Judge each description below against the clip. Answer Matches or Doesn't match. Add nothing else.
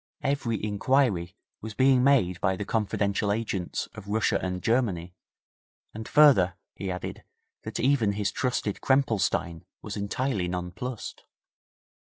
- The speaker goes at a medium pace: Doesn't match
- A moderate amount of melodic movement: Matches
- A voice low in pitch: Matches